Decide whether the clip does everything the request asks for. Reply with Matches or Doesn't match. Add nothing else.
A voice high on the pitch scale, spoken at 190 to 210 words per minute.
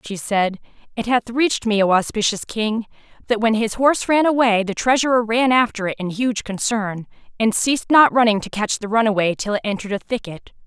Matches